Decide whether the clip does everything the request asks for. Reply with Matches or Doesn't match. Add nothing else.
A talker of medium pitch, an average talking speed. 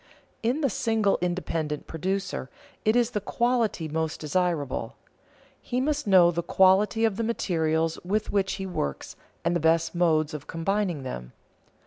Matches